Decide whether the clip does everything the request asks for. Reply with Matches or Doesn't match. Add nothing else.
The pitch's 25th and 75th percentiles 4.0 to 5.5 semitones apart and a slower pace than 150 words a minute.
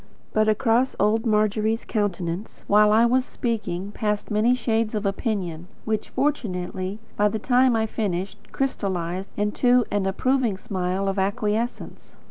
Doesn't match